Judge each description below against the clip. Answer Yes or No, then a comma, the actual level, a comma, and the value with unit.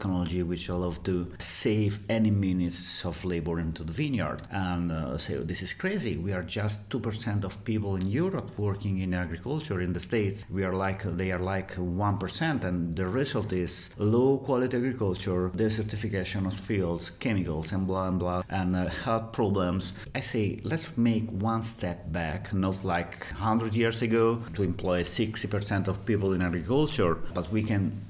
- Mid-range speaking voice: No, very low, 95 Hz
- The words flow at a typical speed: Yes, average, 170 wpm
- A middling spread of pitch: Yes, average, 3.7 semitones